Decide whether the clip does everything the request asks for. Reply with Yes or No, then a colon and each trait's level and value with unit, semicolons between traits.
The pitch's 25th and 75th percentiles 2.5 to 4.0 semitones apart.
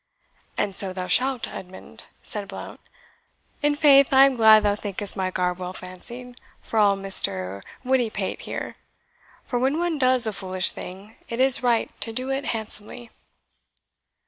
No: average, 5.1 semitones